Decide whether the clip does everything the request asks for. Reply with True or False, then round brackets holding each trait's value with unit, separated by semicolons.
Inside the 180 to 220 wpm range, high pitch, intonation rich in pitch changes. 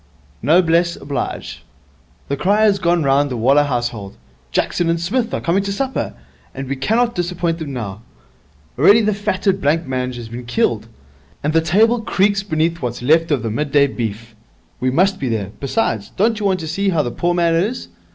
False (190 wpm; 165 Hz; 7.2 semitones)